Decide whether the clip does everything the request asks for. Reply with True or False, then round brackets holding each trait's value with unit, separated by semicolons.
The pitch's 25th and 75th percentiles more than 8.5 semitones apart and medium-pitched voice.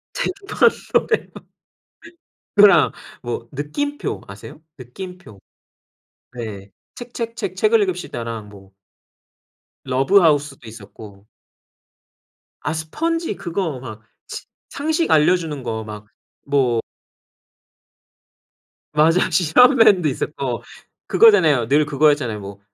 True (8.9 semitones; 150 Hz)